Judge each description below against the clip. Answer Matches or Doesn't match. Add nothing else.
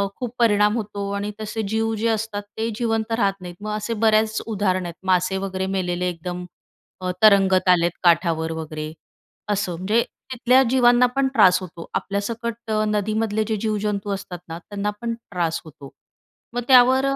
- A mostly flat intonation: Doesn't match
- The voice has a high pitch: Matches